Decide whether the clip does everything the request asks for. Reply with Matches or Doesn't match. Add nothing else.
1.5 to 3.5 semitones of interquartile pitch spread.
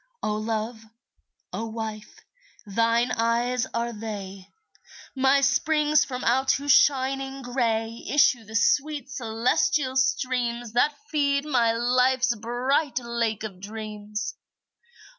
Matches